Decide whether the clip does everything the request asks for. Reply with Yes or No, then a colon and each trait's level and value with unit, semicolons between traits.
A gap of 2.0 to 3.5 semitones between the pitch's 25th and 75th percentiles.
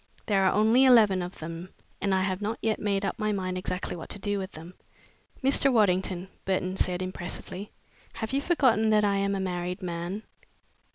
Yes: narrow, 2.6 semitones